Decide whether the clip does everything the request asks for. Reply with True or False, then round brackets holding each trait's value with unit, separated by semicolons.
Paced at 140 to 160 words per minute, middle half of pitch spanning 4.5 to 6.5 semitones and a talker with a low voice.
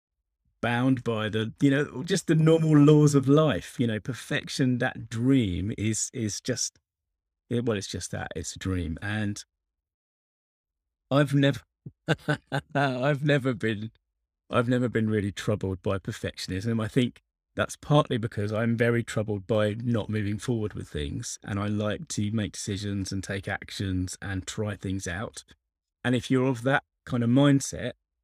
True (155 wpm; 5.1 semitones; 110 Hz)